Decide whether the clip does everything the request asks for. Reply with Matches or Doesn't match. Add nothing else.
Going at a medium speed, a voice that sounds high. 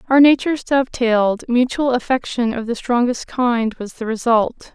Doesn't match